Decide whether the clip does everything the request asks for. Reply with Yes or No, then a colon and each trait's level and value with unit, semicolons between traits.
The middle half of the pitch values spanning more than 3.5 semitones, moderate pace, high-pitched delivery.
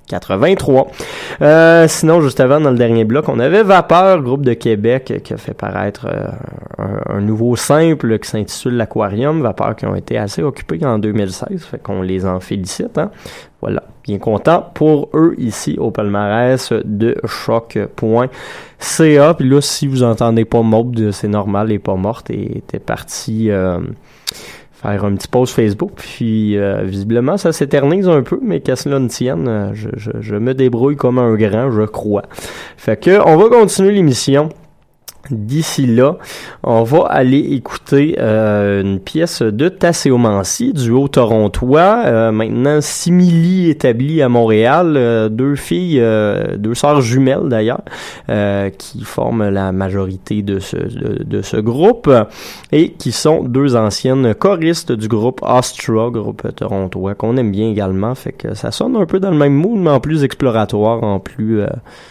No: average, 5.2 semitones; average, 165 wpm; low, 120 Hz